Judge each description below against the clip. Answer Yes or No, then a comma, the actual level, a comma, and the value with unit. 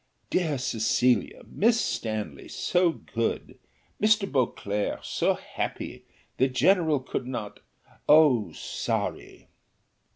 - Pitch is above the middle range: No, low, 130 Hz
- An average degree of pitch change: No, wide, 7.6 semitones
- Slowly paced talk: Yes, slow, 95 wpm